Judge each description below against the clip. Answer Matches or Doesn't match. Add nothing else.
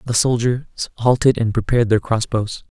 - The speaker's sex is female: Doesn't match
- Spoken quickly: Doesn't match